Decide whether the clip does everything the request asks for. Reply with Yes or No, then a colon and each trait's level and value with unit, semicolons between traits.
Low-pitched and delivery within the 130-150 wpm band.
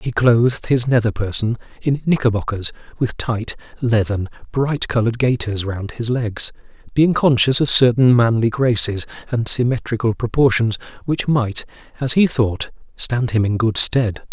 Yes: low, 120 Hz; average, 145 wpm